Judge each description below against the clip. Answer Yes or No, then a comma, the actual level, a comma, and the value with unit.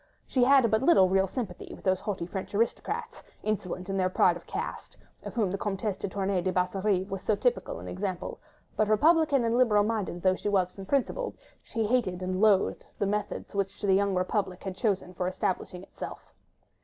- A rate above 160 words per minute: Yes, average, 195 wpm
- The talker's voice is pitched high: Yes, high, 200 Hz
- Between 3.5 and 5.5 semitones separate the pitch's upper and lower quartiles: No, average, 2.9 semitones